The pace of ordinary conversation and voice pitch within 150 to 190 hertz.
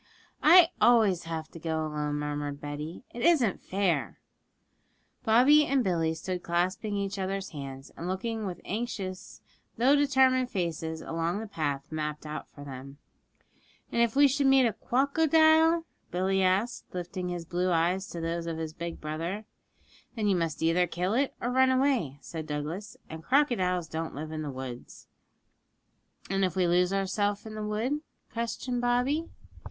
Yes: average, 160 wpm; medium, 185 Hz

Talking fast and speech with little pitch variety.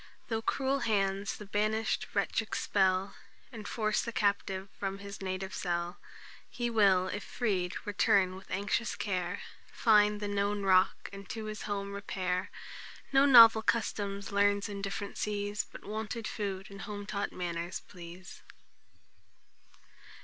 No: average, 140 wpm; narrow, 1.9 semitones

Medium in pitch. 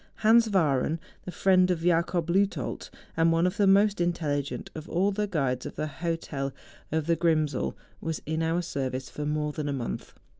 Yes: medium, 165 Hz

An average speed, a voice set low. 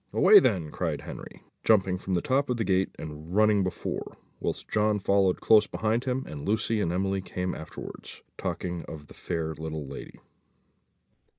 Yes: average, 170 wpm; very low, 95 Hz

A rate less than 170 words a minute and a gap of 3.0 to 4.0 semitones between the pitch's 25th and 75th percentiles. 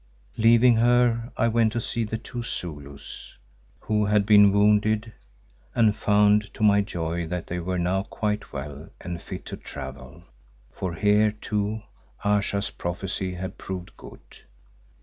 Yes: average, 145 wpm; average, 3.6 semitones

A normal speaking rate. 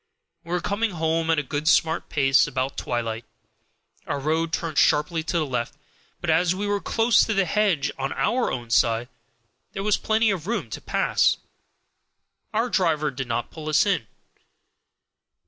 Yes: average, 175 wpm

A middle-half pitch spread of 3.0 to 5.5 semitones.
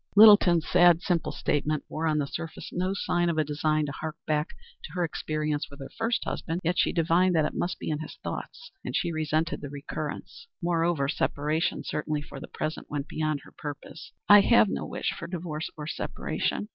No: narrow, 2.5 semitones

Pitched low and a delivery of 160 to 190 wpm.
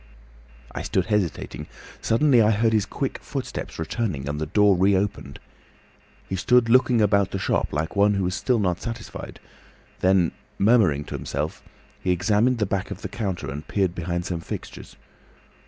Yes: low, 100 Hz; average, 165 wpm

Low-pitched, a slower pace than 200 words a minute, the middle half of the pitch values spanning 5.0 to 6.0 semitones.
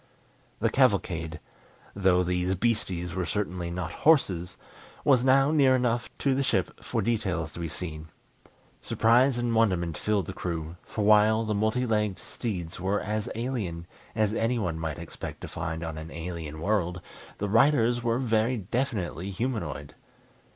Yes: low, 100 Hz; average, 150 wpm; wide, 5.4 semitones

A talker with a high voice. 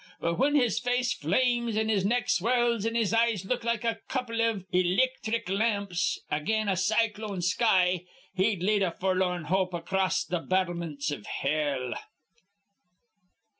Yes: high, 200 Hz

